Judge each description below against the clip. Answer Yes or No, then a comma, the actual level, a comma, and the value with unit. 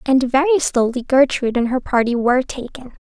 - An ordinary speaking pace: Yes, average, 175 wpm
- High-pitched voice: Yes, very high, 260 Hz